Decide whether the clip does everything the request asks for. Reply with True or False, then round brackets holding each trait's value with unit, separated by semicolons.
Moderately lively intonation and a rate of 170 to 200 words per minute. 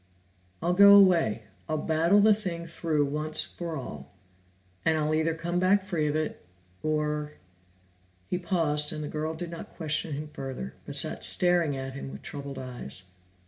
True (3.3 semitones; 175 wpm)